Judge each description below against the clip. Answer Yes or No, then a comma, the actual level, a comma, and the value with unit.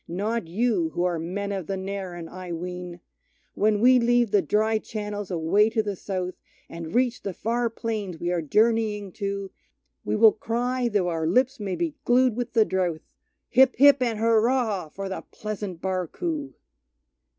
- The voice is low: No, high, 210 Hz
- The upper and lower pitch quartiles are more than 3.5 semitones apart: Yes, average, 4.2 semitones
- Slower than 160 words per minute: No, average, 170 wpm